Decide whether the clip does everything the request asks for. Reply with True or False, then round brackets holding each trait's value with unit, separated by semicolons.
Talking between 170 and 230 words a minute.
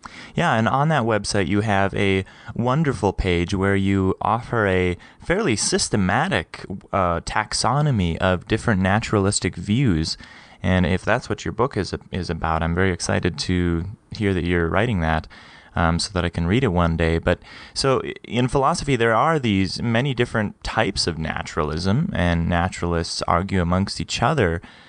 False (160 wpm)